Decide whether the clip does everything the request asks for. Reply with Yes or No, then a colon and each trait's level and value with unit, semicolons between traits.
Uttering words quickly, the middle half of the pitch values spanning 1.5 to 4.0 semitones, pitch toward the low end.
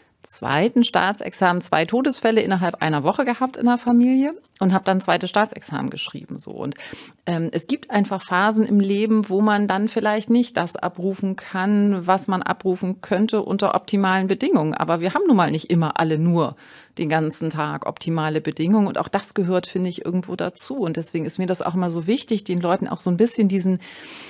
No: fast, 195 wpm; average, 3.5 semitones; high, 190 Hz